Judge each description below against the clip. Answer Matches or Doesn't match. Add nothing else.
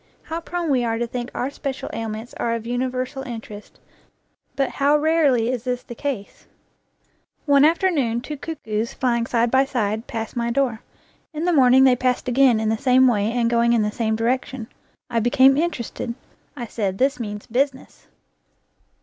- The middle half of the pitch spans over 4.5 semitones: Doesn't match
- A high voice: Matches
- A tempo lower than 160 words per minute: Doesn't match